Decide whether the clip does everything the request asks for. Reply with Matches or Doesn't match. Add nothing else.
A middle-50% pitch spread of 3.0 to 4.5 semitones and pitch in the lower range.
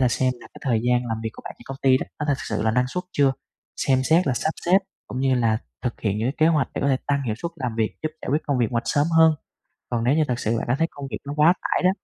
Matches